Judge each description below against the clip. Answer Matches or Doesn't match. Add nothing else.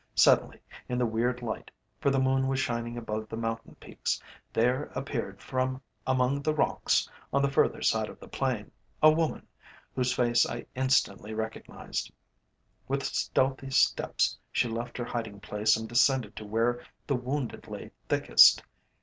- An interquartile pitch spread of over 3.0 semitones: Doesn't match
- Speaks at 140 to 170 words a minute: Matches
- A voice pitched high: Doesn't match